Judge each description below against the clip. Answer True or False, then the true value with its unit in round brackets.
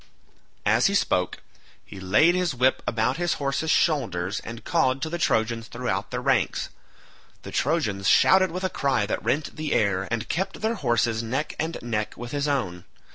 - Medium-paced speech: True (180 wpm)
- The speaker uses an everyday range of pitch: False (6.3 semitones)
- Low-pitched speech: True (130 Hz)